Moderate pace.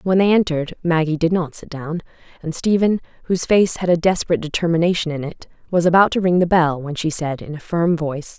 No: fast, 220 wpm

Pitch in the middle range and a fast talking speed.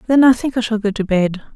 No: high, 225 Hz; fast, 310 wpm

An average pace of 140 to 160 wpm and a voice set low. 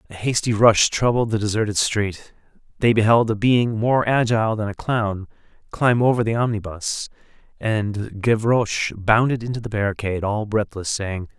Yes: average, 155 wpm; low, 110 Hz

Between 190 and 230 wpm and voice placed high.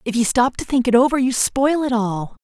No: fast, 270 wpm; high, 245 Hz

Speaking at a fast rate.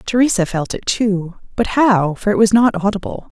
No: average, 175 wpm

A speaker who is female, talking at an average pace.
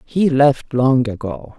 Yes: female; average, 150 wpm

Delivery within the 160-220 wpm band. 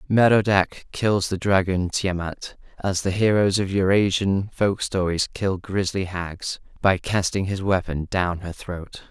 No: average, 150 wpm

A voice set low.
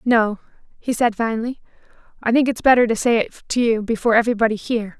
No: high, 230 Hz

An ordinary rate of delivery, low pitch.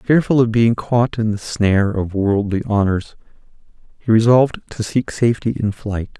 Yes: average, 165 wpm; low, 110 Hz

